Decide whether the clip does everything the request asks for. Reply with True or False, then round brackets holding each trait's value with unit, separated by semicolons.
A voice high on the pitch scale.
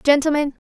True (290 Hz)